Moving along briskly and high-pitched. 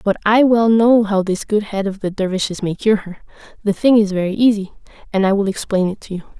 Yes: fast, 245 wpm; high, 205 Hz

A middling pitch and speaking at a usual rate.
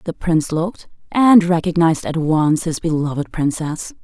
Yes: medium, 165 Hz; average, 150 wpm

